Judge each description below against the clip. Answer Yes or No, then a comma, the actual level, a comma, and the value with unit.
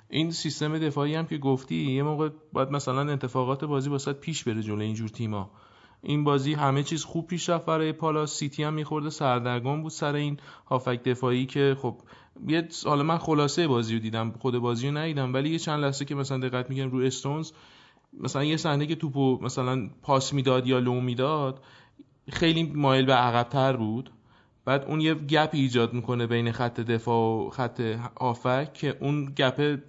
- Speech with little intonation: No, average, 3.3 semitones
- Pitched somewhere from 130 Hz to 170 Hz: Yes, low, 135 Hz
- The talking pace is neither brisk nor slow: No, fast, 180 wpm